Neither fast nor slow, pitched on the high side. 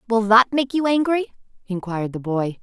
Yes: average, 185 wpm; high, 225 Hz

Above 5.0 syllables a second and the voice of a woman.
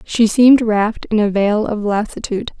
Yes: 5.4 syllables/s; female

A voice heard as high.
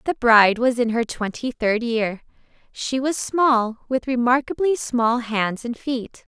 Yes: high, 240 Hz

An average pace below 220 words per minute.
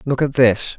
No: fast, 230 wpm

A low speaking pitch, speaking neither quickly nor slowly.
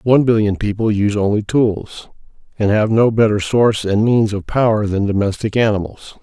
Yes: low, 105 Hz; average, 175 wpm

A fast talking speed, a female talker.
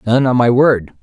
No: fast, 235 wpm; male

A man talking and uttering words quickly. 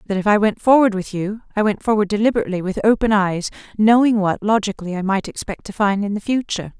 No: female; fast, 220 wpm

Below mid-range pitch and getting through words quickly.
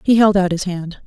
No: high, 190 Hz; fast, 280 wpm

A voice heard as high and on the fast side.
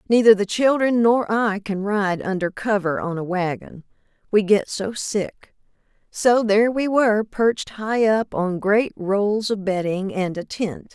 No: high, 210 Hz; average, 170 wpm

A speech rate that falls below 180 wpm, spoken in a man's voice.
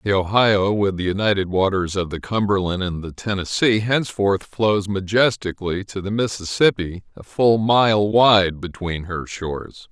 Yes: average, 150 wpm; male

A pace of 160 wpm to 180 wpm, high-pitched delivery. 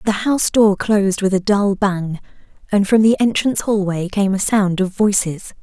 No: average, 190 wpm; high, 200 Hz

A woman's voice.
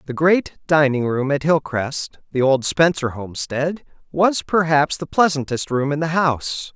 No: male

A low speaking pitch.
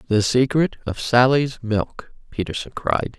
Yes: low, 120 Hz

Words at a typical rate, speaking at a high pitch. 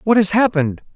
Yes: average, 190 wpm; high, 205 Hz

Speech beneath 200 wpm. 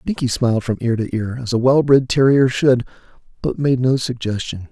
No: fast, 205 wpm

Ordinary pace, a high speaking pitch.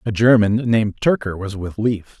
No: average, 190 wpm; low, 110 Hz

